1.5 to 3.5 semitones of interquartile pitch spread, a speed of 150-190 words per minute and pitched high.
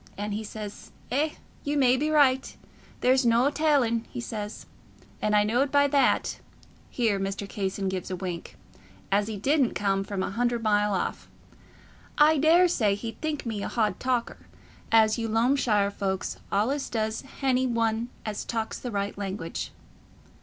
No: average, 4.2 semitones; average, 155 wpm; high, 225 Hz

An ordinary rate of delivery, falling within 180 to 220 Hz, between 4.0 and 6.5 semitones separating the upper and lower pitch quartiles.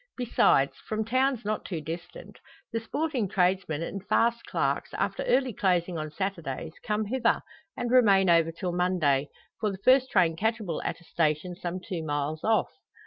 Yes: average, 165 wpm; medium, 185 Hz; average, 5.2 semitones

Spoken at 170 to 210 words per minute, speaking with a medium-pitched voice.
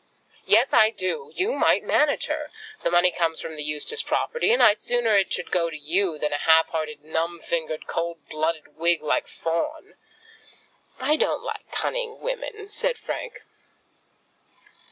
No: average, 160 wpm; medium, 175 Hz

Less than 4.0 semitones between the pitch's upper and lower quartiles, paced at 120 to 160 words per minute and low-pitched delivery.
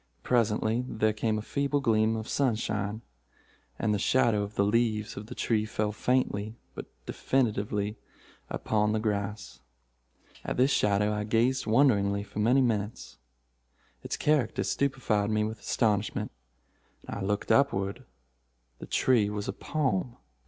Yes: narrow, 2.5 semitones; average, 140 wpm; low, 110 Hz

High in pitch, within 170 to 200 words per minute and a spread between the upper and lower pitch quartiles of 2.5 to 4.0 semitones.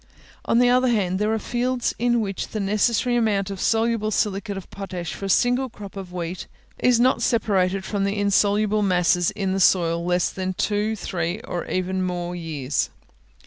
Yes: high, 200 Hz; average, 185 wpm; average, 3.4 semitones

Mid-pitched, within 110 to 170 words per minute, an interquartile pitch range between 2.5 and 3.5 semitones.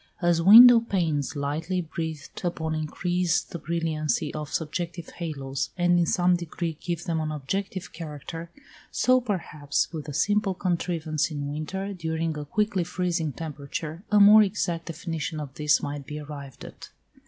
Yes: medium, 165 Hz; average, 155 wpm; average, 2.9 semitones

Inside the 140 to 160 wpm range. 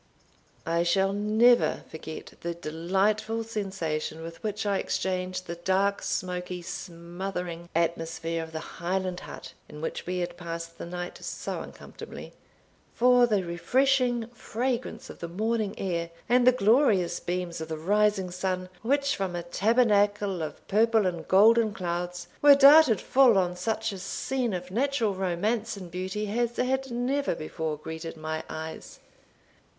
Yes: average, 145 wpm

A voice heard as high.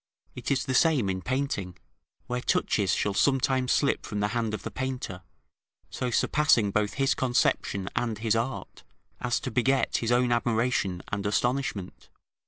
No: low, 120 Hz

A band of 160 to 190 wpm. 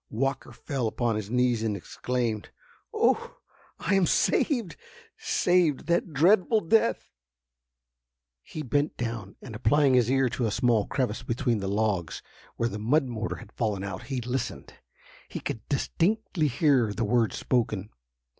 No: average, 145 wpm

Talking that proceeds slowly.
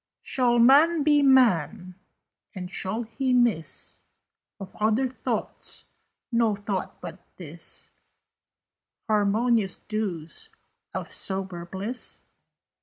Yes: slow, 95 wpm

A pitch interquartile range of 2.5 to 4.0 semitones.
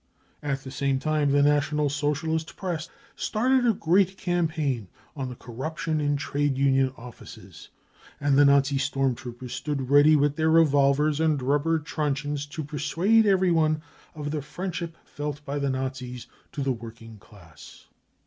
Yes: average, 2.8 semitones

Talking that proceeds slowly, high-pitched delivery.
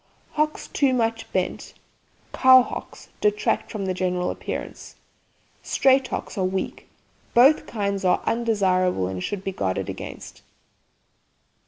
Yes: slow, 125 wpm; high, 205 Hz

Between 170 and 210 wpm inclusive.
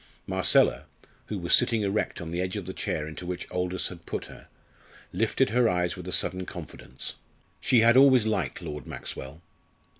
Yes: average, 180 wpm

